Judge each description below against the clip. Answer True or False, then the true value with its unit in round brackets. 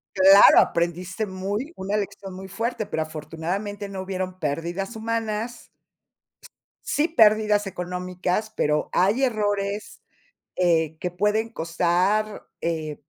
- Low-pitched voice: False (195 Hz)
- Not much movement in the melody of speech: False (3.2 semitones)